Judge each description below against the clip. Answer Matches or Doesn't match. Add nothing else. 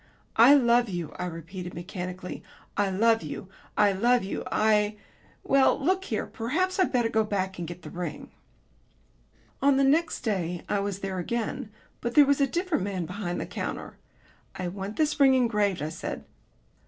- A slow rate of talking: Doesn't match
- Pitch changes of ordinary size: Doesn't match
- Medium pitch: Doesn't match